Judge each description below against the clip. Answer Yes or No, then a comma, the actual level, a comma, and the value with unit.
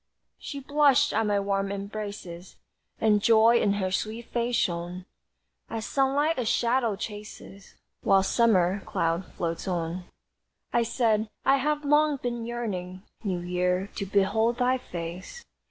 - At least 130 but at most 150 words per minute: Yes, average, 140 wpm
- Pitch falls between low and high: No, high, 210 Hz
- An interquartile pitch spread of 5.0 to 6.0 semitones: No, average, 4.3 semitones